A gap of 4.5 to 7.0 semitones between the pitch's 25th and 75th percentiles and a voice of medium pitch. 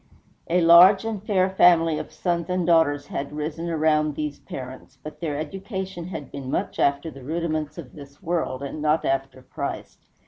No: average, 3.2 semitones; medium, 155 Hz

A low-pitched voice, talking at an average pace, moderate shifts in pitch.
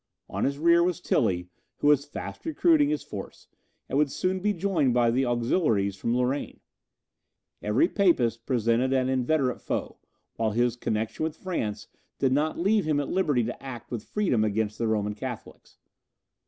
No: low, 130 Hz; average, 170 wpm; wide, 6.1 semitones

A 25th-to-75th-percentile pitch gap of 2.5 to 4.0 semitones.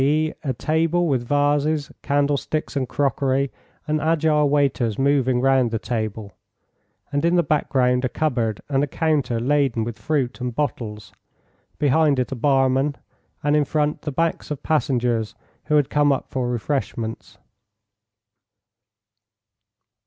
Yes: average, 3.3 semitones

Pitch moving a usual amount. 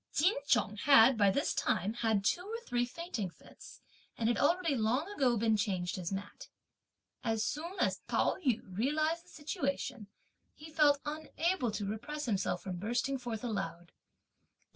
No: wide, 6.0 semitones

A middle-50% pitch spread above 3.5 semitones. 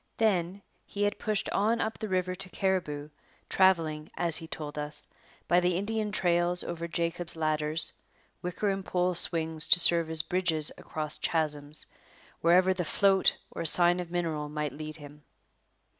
No: average, 3.2 semitones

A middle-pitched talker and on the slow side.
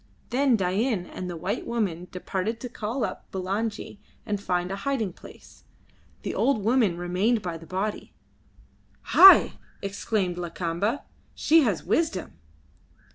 No: high, 200 Hz; slow, 130 wpm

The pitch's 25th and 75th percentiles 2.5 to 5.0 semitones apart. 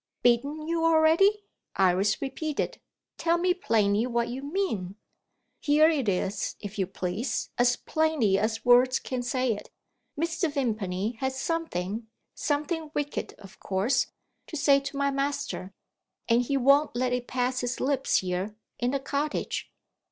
No: wide, 5.4 semitones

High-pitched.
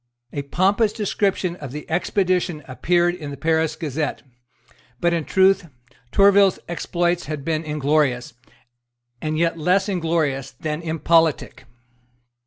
No: medium, 165 Hz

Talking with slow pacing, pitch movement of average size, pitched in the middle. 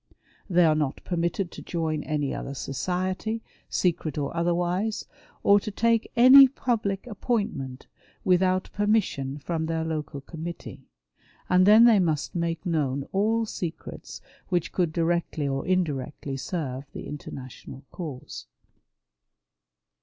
Yes: slow, 125 wpm; average, 4.8 semitones; medium, 170 Hz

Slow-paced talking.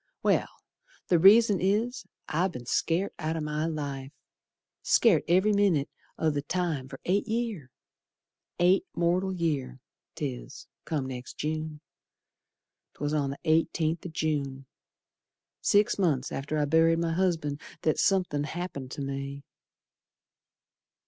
Yes: slow, 130 wpm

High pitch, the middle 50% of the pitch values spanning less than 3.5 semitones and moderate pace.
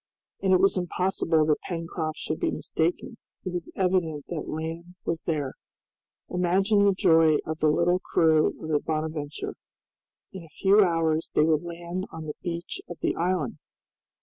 No: medium, 165 Hz; narrow, 2.4 semitones; average, 165 wpm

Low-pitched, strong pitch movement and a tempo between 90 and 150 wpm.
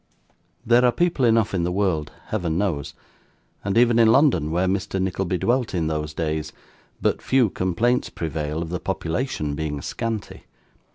No: very low, 95 Hz; wide, 6.3 semitones; average, 160 wpm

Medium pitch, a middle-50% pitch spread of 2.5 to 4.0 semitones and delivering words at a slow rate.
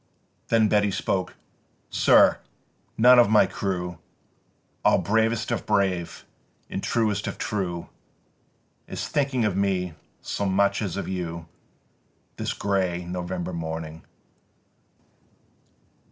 No: very low, 95 Hz; average, 3.3 semitones; slow, 110 wpm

